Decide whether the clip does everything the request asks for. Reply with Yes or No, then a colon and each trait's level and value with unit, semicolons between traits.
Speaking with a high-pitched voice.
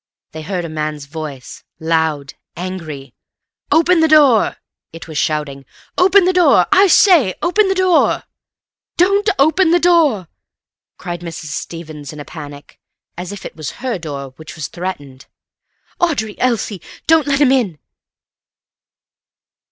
No: medium, 180 Hz